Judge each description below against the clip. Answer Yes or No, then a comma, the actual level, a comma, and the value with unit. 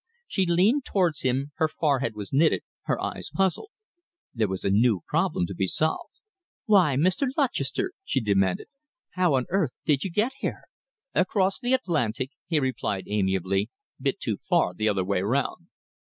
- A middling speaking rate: Yes, average, 165 wpm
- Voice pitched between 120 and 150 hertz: Yes, medium, 140 Hz